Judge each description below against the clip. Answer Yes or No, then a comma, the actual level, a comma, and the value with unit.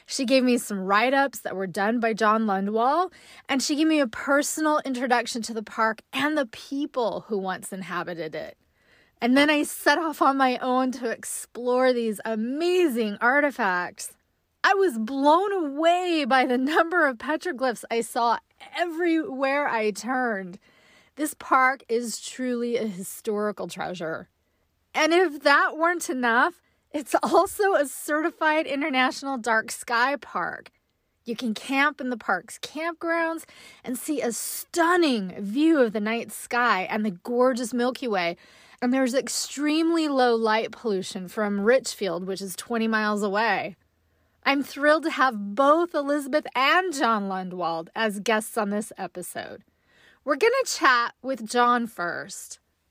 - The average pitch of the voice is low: No, very high, 250 Hz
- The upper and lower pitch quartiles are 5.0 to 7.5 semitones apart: Yes, average, 5.3 semitones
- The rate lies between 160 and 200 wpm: No, average, 150 wpm